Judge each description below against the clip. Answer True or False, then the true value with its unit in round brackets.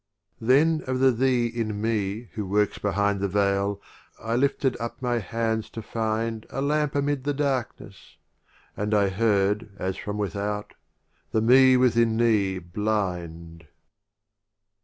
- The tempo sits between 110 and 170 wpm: True (145 wpm)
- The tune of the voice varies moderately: True (3.6 semitones)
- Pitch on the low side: True (110 Hz)